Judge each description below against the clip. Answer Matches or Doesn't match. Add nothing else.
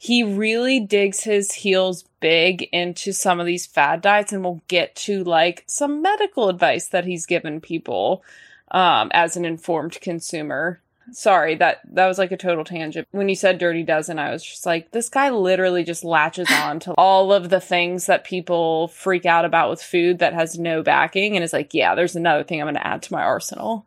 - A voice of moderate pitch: Matches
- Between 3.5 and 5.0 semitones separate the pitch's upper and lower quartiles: Doesn't match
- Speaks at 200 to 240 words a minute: Matches